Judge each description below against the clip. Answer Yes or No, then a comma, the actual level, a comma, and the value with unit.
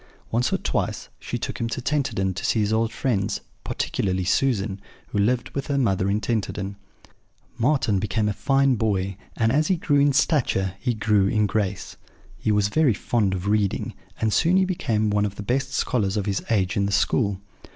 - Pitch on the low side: Yes, low, 110 Hz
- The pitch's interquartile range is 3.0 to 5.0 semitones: Yes, average, 4.5 semitones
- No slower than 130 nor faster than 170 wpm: No, average, 195 wpm